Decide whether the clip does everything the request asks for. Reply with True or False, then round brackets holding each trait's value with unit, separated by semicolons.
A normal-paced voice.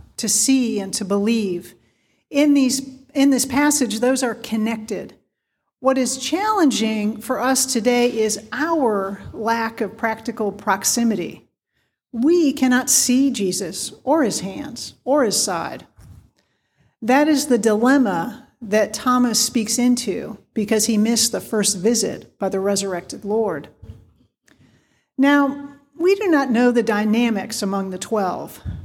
False (130 wpm)